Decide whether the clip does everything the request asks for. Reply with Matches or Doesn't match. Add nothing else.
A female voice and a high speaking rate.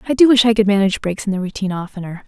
Matches